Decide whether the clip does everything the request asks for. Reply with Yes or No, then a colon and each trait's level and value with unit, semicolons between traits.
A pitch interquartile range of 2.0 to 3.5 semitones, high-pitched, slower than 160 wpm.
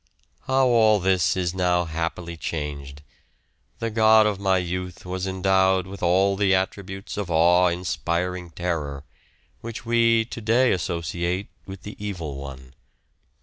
No: average, 2.9 semitones; very low, 90 Hz; average, 140 wpm